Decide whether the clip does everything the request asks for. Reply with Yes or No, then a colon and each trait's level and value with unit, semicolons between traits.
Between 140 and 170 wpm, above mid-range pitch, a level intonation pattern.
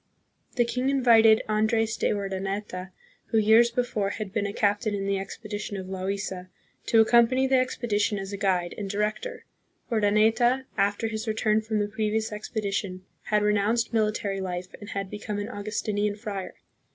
Yes: average, 165 wpm; high, 210 Hz; narrow, 2.0 semitones